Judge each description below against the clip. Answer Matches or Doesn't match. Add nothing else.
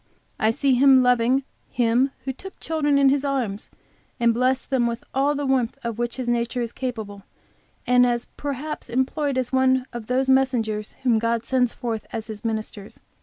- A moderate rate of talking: Matches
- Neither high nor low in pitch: Doesn't match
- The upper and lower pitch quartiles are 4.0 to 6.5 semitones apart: Doesn't match